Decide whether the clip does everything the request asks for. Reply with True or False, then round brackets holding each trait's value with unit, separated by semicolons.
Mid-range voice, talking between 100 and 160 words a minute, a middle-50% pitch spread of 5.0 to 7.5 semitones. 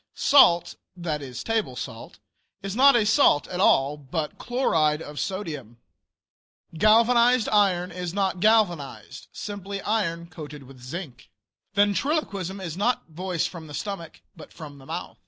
True (180 Hz; 140 wpm; 5.5 semitones)